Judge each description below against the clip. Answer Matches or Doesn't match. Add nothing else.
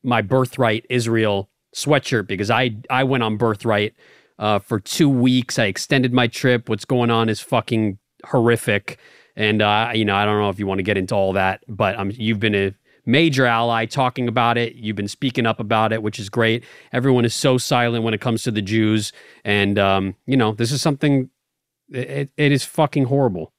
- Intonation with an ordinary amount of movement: Matches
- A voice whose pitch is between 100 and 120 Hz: Matches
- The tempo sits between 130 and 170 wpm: Doesn't match